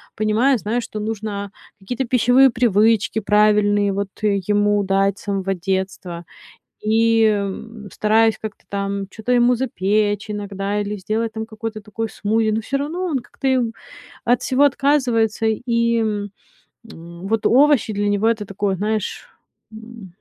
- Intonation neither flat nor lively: No, narrow, 2.2 semitones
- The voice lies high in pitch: Yes, high, 215 Hz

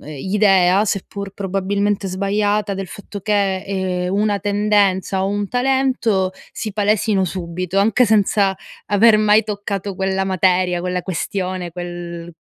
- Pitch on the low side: No, high, 195 Hz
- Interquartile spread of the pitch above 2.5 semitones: No, narrow, 1.8 semitones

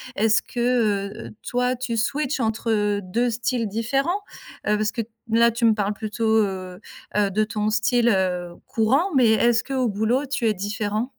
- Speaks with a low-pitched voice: No, high, 225 Hz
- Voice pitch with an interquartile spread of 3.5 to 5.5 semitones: No, average, 2.9 semitones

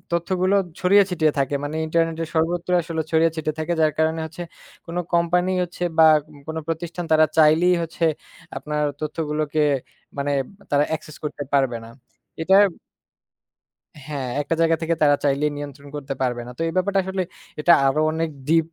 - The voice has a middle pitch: Yes, medium, 160 Hz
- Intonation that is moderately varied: No, narrow, 2.3 semitones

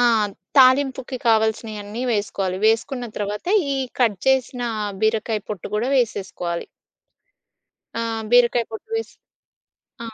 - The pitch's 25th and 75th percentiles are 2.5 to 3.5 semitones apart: Yes, average, 2.9 semitones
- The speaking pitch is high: Yes, high, 225 Hz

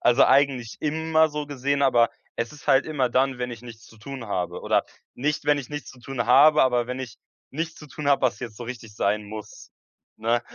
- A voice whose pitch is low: Yes, low, 130 Hz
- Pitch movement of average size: Yes, average, 3.5 semitones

